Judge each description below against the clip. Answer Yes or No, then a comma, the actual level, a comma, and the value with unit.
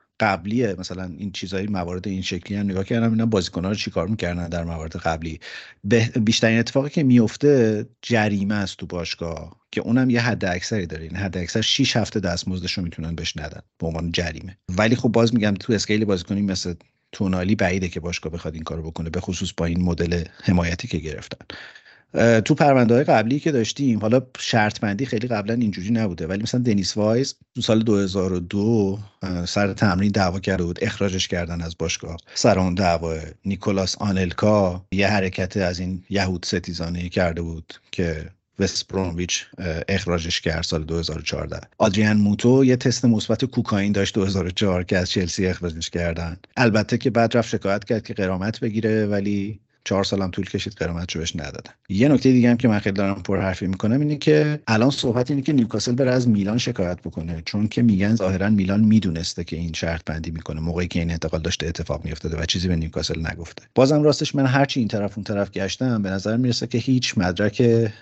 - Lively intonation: No, average, 4.4 semitones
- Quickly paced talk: Yes, fast, 185 wpm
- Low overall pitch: Yes, low, 100 Hz